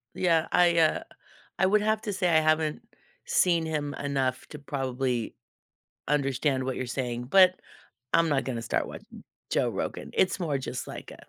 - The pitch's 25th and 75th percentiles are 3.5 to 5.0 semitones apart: Yes, average, 4.6 semitones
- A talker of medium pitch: Yes, medium, 150 Hz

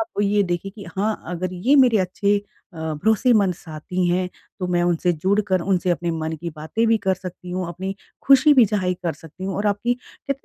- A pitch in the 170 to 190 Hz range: Yes, medium, 185 Hz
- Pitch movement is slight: No, average, 3.1 semitones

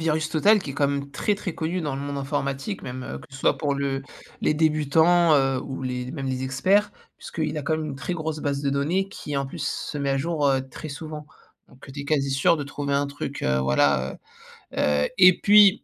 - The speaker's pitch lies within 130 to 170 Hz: Yes, medium, 140 Hz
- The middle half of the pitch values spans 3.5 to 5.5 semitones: No, average, 2.7 semitones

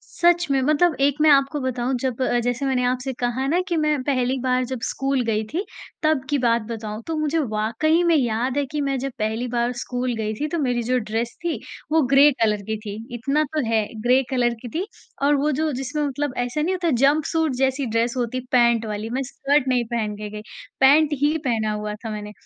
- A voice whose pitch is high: Yes, very high, 255 Hz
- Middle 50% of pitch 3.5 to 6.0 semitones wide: Yes, average, 3.8 semitones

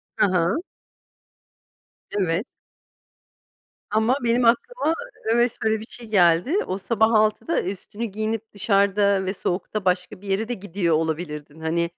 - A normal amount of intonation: Yes, average, 3.7 semitones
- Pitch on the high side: Yes, high, 200 Hz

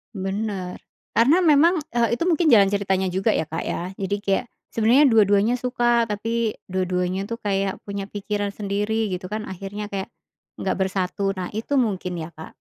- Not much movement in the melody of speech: No, average, 3.2 semitones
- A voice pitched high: Yes, high, 205 Hz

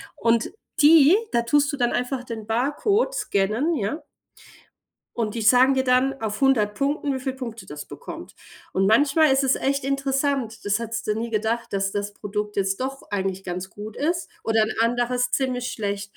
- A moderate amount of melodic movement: Yes, average, 4.4 semitones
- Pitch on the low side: No, high, 240 Hz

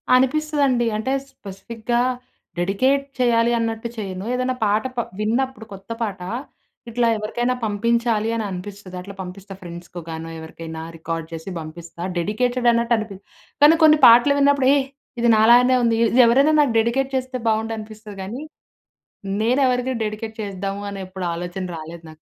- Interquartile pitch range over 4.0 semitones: Yes, average, 4.4 semitones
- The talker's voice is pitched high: Yes, high, 220 Hz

